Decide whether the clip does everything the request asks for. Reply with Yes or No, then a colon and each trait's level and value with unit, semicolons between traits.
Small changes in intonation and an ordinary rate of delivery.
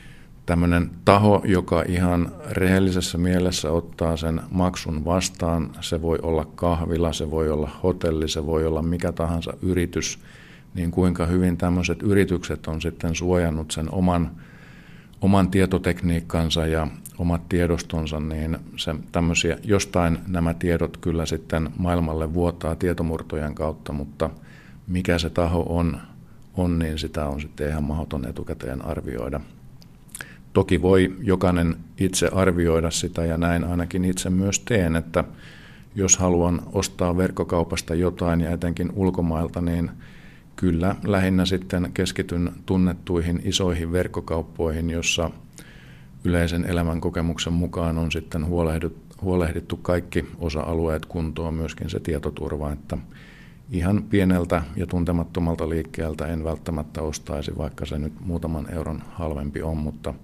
Yes: narrow, 1.9 semitones; average, 125 wpm